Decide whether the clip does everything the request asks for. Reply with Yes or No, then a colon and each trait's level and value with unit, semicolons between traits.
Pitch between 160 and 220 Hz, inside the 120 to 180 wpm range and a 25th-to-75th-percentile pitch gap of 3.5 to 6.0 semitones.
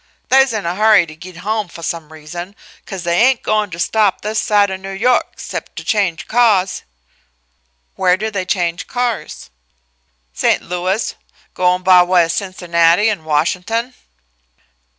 Yes: medium, 185 Hz; average, 155 wpm; average, 3.8 semitones